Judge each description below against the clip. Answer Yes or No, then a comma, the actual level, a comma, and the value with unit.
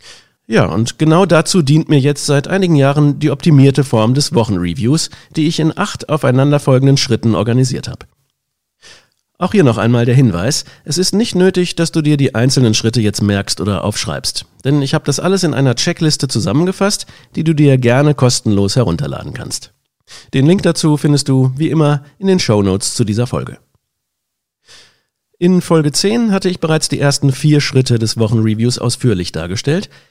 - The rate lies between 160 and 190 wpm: Yes, average, 170 wpm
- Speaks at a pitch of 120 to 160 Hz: Yes, medium, 140 Hz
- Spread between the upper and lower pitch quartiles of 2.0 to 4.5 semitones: No, average, 4.9 semitones